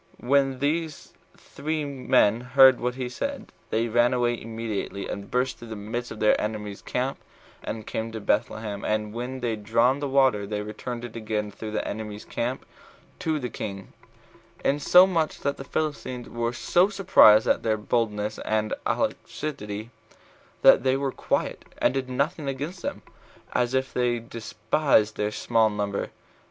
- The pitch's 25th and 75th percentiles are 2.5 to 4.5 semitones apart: Yes, average, 3.8 semitones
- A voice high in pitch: No, low, 120 Hz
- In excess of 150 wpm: Yes, average, 160 wpm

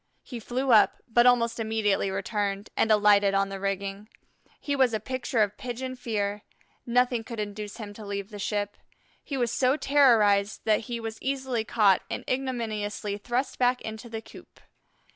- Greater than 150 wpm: Yes, average, 170 wpm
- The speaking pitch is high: Yes, high, 220 Hz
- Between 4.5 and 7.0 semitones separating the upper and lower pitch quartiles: No, average, 3.3 semitones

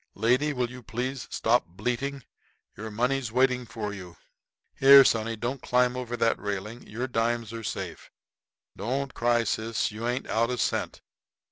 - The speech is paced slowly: No, average, 155 wpm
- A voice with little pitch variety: Yes, narrow, 2.2 semitones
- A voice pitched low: Yes, low, 120 Hz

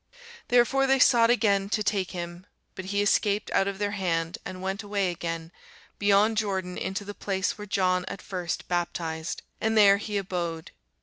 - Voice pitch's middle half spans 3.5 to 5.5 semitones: No, narrow, 2.4 semitones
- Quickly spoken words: No, average, 175 wpm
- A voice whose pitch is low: No, high, 195 Hz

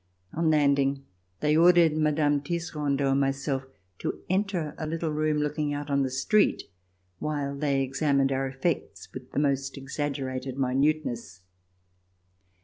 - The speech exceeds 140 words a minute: No, slow, 135 wpm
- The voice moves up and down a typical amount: No, narrow, 2.2 semitones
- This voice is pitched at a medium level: Yes, medium, 145 Hz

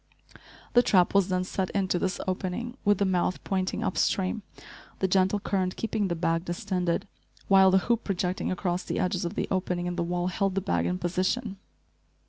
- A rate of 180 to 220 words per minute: Yes, average, 190 wpm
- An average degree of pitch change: No, narrow, 1.7 semitones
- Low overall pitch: No, medium, 185 Hz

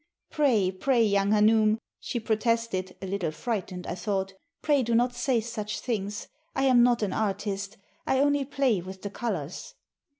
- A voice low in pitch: No, high, 215 Hz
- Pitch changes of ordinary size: Yes, average, 3.7 semitones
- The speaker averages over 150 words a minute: Yes, average, 165 wpm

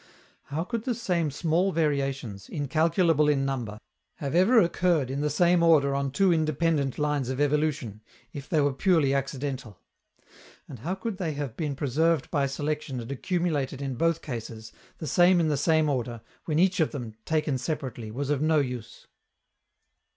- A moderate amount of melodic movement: Yes, average, 3.6 semitones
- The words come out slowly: No, average, 170 wpm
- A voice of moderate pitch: Yes, medium, 145 Hz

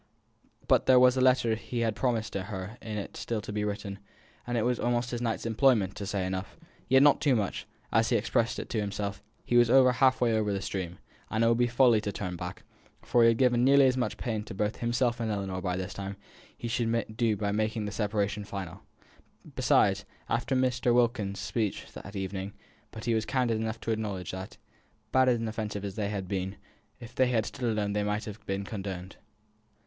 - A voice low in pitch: Yes, low, 110 Hz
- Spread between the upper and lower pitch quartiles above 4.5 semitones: No, average, 3.1 semitones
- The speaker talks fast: Yes, fast, 215 wpm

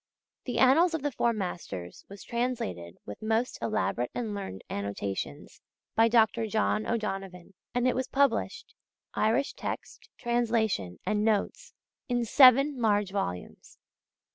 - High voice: Yes, high, 220 Hz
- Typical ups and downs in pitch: Yes, average, 4.2 semitones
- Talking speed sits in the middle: No, slow, 130 wpm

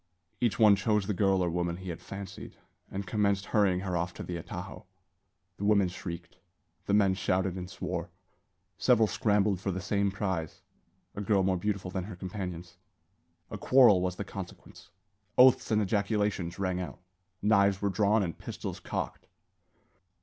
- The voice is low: Yes, very low, 95 Hz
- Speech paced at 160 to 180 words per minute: Yes, average, 165 wpm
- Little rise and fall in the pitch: Yes, narrow, 2.2 semitones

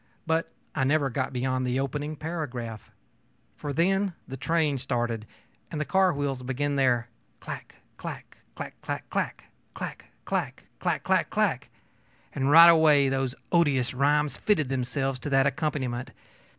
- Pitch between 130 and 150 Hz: Yes, medium, 140 Hz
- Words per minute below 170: Yes, average, 145 wpm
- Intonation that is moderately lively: Yes, average, 3.2 semitones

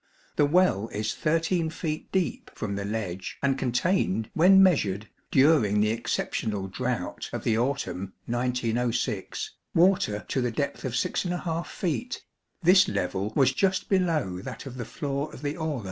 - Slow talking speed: No, average, 150 wpm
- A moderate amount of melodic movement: No, wide, 7.2 semitones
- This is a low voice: Yes, low, 130 Hz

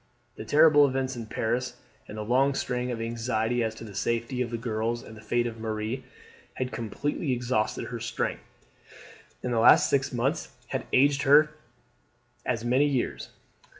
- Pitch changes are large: No, average, 2.8 semitones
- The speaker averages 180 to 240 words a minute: No, average, 170 wpm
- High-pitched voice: No, low, 120 Hz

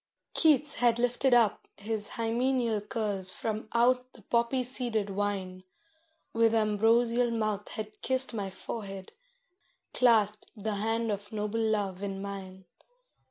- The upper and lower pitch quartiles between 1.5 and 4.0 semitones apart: Yes, narrow, 2.6 semitones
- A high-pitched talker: Yes, high, 220 Hz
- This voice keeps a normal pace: No, slow, 125 wpm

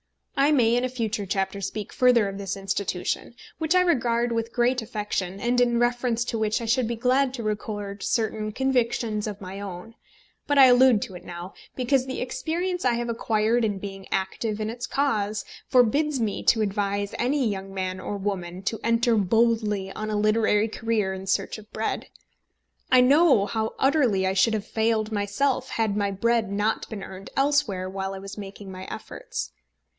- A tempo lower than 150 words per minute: No, average, 185 wpm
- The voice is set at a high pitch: Yes, high, 220 Hz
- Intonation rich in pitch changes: No, average, 3.5 semitones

